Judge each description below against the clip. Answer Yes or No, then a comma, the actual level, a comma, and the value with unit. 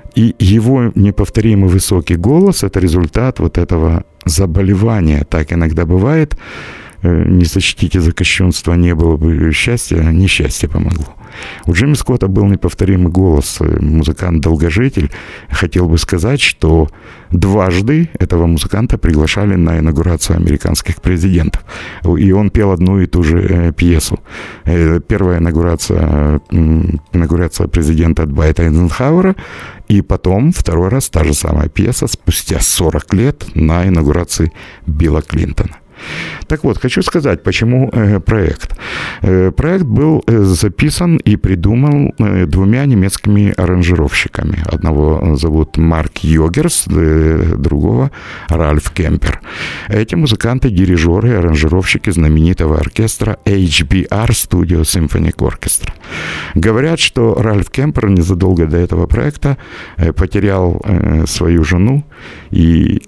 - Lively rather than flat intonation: No, average, 4.2 semitones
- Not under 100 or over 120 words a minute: Yes, slow, 110 wpm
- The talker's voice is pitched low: Yes, very low, 90 Hz